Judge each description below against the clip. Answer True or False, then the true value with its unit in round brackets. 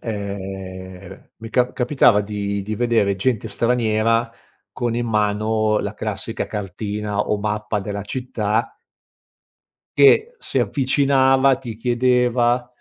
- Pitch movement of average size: True (3.1 semitones)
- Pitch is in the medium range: False (110 Hz)